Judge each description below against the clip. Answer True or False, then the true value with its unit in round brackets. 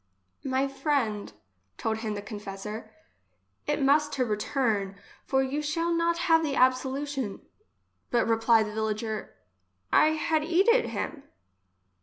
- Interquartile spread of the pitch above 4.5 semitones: True (5.6 semitones)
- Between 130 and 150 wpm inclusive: True (140 wpm)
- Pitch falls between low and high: False (260 Hz)